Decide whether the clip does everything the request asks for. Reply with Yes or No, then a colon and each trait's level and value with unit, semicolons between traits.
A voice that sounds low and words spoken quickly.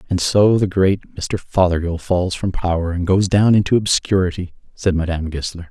No: very low, 90 Hz; average, 180 wpm